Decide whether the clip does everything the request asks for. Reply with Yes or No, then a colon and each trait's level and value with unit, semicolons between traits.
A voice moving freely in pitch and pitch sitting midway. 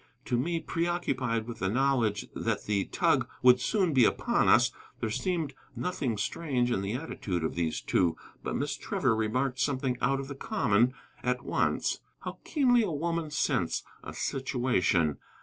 No: wide, 5.9 semitones; low, 125 Hz